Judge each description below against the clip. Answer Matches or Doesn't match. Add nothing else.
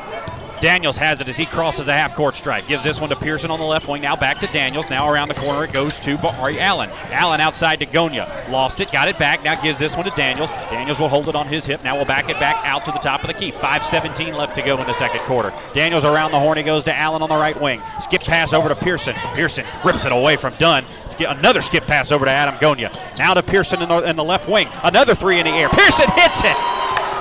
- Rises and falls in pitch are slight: Matches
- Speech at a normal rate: Doesn't match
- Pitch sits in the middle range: Matches